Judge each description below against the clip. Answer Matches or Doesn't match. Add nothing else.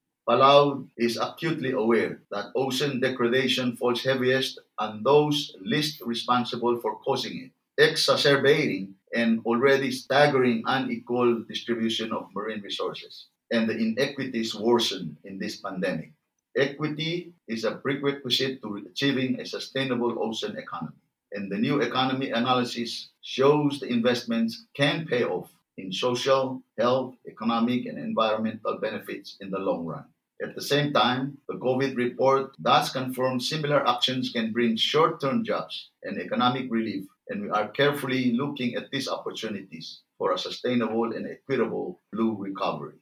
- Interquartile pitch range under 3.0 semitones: Matches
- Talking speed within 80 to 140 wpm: Matches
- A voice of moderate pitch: Doesn't match